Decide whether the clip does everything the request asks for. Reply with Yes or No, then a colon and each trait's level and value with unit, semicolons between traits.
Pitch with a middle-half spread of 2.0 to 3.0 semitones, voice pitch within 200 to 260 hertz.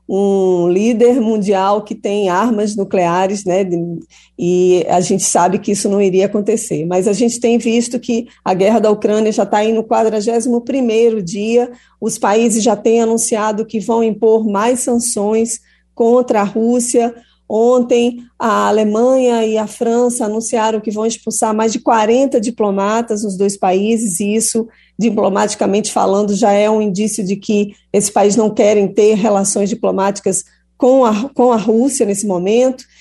Yes: narrow, 2.4 semitones; high, 220 Hz